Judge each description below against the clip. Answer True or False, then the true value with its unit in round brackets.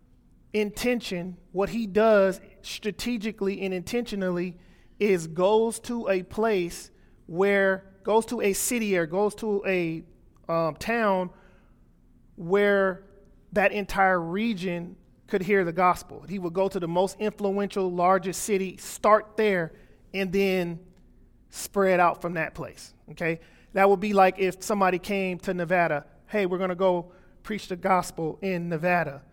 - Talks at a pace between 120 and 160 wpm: True (140 wpm)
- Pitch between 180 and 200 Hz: True (190 Hz)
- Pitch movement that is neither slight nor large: False (2.2 semitones)